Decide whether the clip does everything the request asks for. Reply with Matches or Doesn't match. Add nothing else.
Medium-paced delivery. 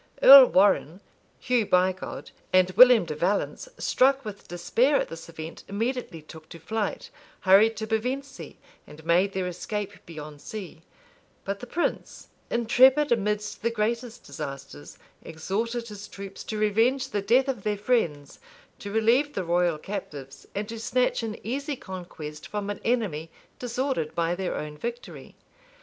Matches